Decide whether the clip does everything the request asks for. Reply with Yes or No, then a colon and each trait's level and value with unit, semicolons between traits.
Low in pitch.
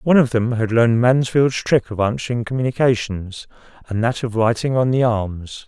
Yes: low, 120 Hz